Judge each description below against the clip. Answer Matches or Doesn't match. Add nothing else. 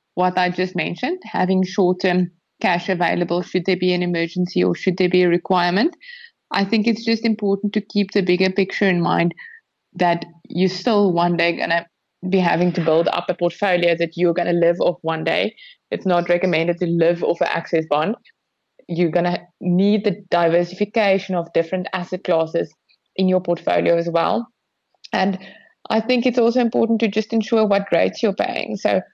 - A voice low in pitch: Doesn't match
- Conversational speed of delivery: Matches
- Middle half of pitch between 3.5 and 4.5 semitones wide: Doesn't match